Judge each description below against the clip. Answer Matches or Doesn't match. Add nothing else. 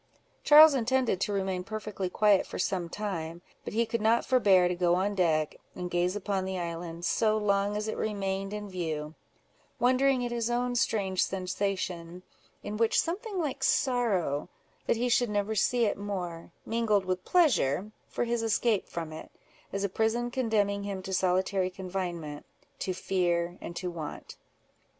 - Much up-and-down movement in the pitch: Doesn't match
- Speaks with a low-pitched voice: Doesn't match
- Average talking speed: Matches